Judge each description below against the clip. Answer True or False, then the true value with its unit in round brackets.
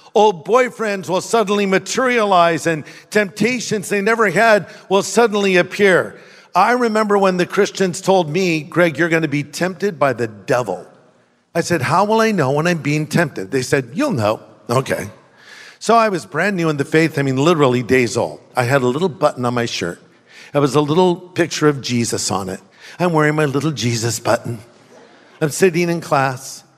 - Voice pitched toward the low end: False (170 Hz)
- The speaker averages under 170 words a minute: False (190 wpm)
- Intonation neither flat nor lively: False (5.8 semitones)